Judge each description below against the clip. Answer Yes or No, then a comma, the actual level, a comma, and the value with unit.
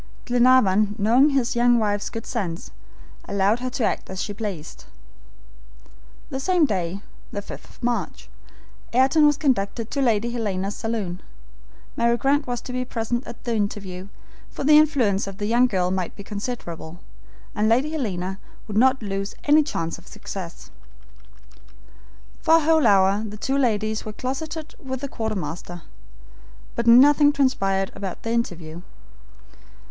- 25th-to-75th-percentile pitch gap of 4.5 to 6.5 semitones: Yes, average, 4.8 semitones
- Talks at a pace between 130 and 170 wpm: Yes, average, 150 wpm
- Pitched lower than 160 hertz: No, high, 225 Hz